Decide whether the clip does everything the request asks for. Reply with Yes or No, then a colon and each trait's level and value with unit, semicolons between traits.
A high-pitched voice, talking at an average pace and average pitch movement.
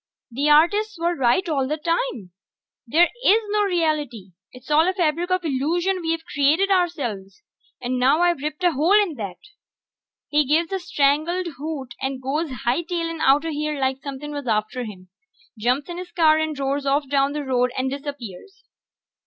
Yes: very high, 300 Hz; average, 170 wpm; average, 4.4 semitones